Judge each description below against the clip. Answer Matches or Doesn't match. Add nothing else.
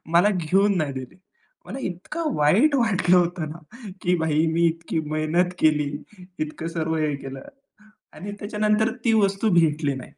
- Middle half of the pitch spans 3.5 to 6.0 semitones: Matches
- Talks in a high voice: Doesn't match